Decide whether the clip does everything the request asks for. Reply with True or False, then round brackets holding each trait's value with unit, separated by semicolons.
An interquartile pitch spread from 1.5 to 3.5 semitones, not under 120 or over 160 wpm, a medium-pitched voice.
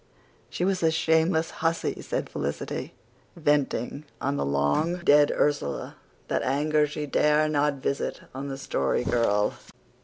True (3.1 semitones; 140 wpm; 150 Hz)